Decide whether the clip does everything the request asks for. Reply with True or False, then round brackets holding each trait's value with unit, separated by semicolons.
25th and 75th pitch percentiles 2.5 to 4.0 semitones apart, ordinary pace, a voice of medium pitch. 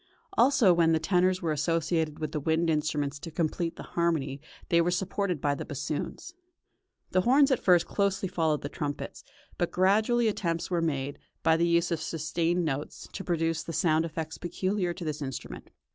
True (2.8 semitones; 180 wpm; 165 Hz)